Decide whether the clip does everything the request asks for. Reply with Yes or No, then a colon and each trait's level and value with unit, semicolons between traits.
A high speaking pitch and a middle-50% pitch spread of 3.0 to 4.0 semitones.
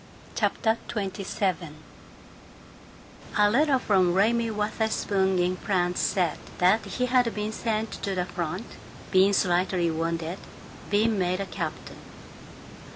Yes: high, 195 Hz; average, 3.4 semitones